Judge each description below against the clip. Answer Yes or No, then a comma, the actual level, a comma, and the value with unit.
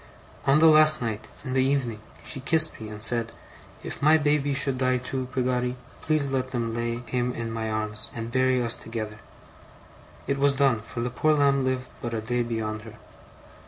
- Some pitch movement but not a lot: Yes, average, 3.2 semitones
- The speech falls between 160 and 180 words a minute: No, average, 195 wpm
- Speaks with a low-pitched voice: Yes, low, 125 Hz